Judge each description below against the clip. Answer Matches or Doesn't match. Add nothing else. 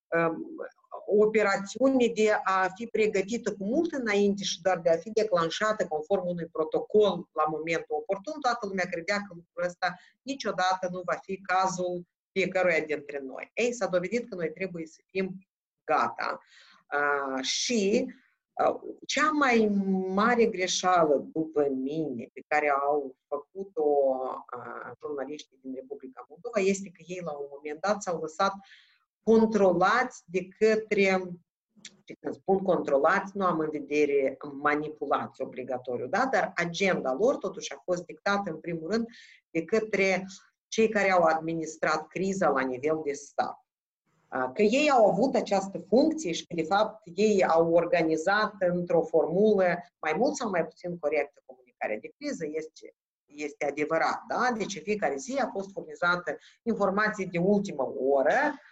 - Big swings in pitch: Doesn't match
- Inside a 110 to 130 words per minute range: Doesn't match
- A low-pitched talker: Doesn't match